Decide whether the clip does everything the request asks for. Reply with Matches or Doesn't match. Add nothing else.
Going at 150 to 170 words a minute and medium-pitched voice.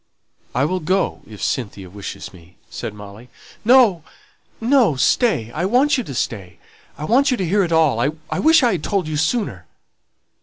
Doesn't match